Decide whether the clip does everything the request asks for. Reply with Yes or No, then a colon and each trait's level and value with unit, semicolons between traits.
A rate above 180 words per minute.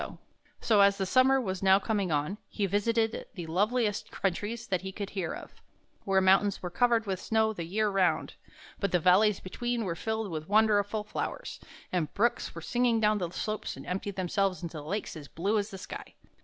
Yes: average, 195 wpm